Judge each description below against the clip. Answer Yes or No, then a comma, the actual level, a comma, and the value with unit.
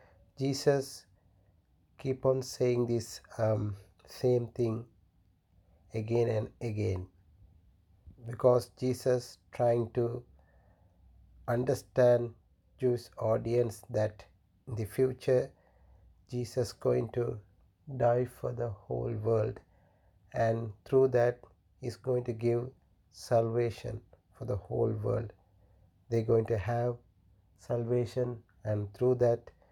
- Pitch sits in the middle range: No, low, 115 Hz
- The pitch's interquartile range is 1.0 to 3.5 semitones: No, average, 4.4 semitones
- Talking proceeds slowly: Yes, slow, 100 wpm